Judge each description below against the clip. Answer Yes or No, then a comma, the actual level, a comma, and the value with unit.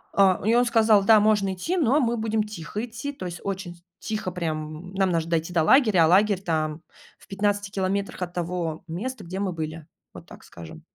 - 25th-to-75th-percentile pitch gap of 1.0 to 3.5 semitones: No, average, 4.2 semitones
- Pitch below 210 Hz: Yes, high, 190 Hz